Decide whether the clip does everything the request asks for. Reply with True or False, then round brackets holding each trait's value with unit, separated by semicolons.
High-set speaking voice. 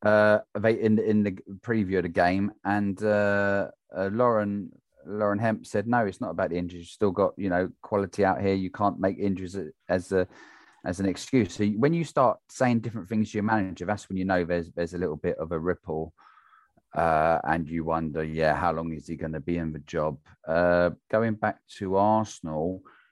False (95 Hz)